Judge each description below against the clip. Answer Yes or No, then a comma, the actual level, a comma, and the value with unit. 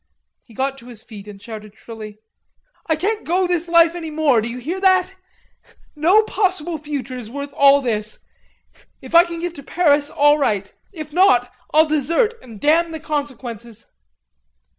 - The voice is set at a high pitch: Yes, very high, 290 Hz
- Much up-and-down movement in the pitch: Yes, wide, 6.0 semitones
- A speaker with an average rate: Yes, average, 170 wpm